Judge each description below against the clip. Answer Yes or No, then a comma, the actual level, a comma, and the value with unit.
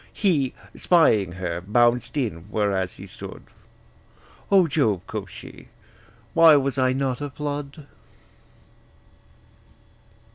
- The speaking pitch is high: No, low, 130 Hz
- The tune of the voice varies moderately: No, wide, 6.5 semitones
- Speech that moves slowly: Yes, slow, 105 wpm